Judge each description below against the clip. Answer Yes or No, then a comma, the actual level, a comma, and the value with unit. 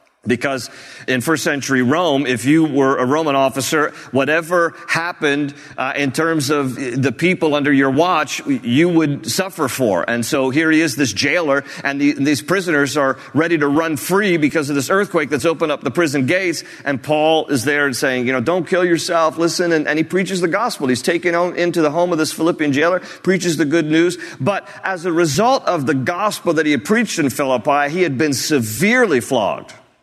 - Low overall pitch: No, medium, 155 Hz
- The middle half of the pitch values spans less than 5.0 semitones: Yes, average, 3.7 semitones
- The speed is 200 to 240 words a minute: Yes, fast, 205 wpm